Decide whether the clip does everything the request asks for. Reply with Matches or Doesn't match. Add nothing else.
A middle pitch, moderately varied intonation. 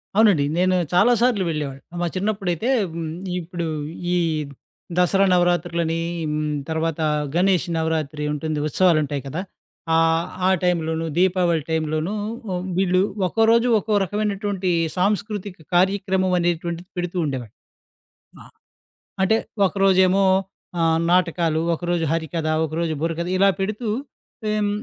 Matches